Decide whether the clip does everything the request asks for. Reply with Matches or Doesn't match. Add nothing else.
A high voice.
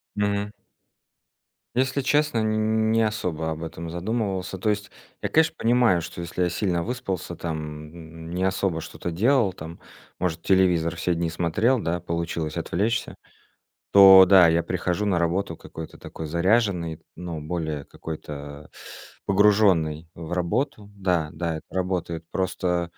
Doesn't match